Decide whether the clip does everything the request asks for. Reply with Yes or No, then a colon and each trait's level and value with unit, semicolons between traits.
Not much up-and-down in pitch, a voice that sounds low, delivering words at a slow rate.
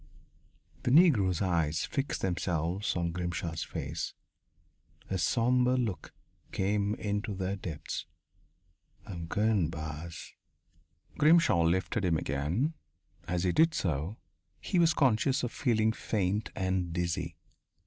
No: average, 5.1 semitones; very low, 95 Hz; slow, 115 wpm